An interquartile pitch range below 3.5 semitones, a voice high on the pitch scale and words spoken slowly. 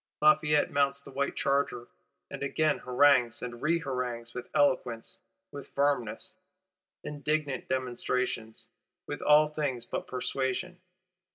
No: average, 3.0 semitones; medium, 140 Hz; slow, 110 wpm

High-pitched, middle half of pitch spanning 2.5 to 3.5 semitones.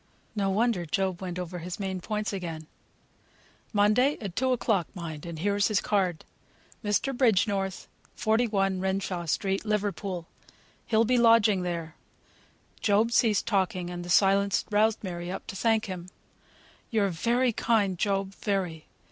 Yes: high, 195 Hz; average, 3.1 semitones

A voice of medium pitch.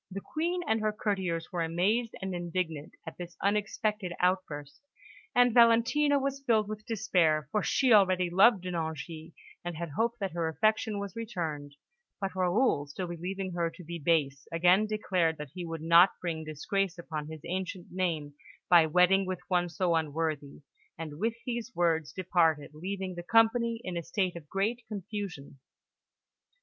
Yes: medium, 180 Hz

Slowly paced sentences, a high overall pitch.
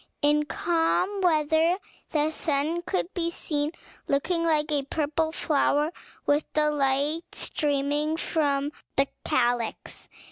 Yes: slow, 115 wpm; very high, 300 Hz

